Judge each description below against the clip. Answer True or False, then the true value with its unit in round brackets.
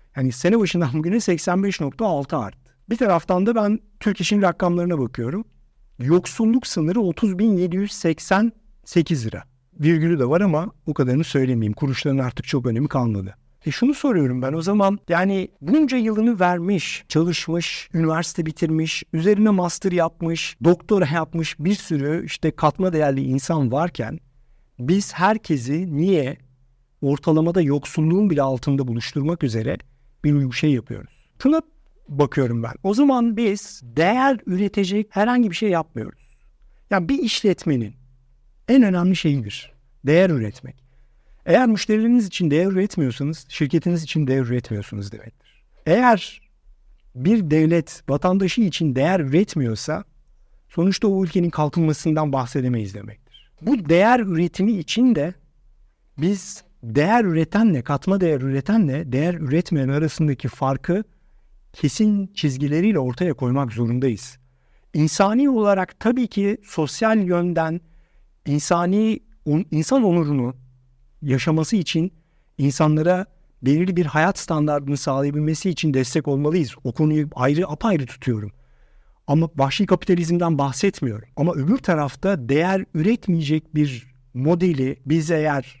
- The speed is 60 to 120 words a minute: True (115 wpm)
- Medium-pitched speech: True (160 Hz)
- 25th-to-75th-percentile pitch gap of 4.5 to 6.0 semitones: True (5.6 semitones)